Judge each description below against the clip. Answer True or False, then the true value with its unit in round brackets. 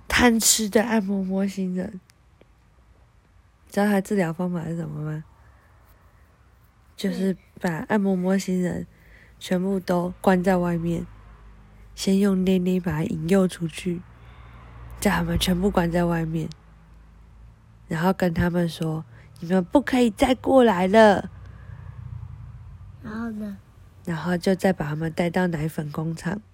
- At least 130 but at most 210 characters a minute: True (190 characters per minute)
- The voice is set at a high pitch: False (175 Hz)